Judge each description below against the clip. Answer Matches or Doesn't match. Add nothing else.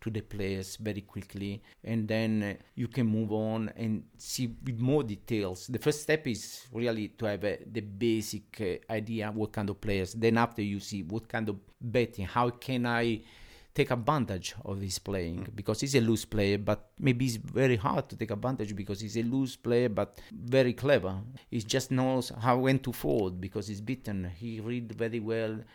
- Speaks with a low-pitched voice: Matches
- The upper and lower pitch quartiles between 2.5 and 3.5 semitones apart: Matches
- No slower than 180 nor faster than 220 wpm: Matches